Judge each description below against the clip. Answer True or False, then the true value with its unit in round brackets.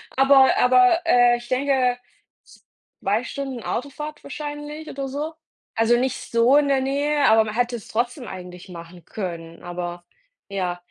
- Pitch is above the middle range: True (245 Hz)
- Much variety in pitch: True (6.0 semitones)